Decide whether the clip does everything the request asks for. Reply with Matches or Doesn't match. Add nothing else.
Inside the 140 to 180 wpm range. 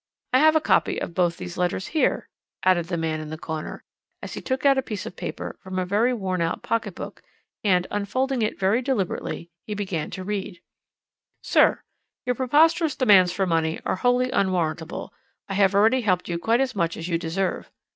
Doesn't match